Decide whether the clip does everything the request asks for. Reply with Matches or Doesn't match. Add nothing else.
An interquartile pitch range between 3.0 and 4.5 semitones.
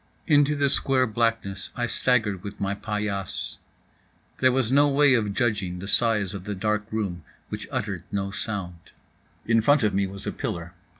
Matches